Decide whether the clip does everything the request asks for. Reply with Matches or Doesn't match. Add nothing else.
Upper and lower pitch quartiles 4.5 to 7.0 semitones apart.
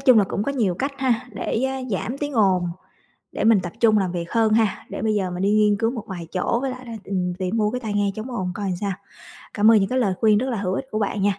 Doesn't match